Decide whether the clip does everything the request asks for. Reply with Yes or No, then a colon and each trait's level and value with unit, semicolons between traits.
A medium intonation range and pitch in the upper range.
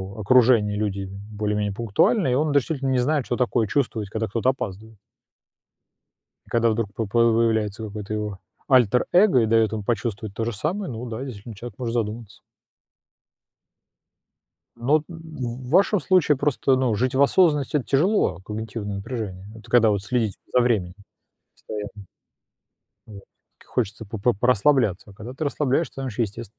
No: average, 3.9 semitones; low, 115 Hz